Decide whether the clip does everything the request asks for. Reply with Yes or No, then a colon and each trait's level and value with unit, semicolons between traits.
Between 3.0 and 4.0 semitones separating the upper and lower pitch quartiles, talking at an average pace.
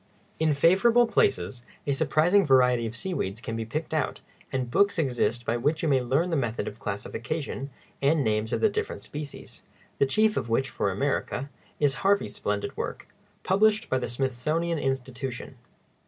No: wide, 5.4 semitones; average, 170 wpm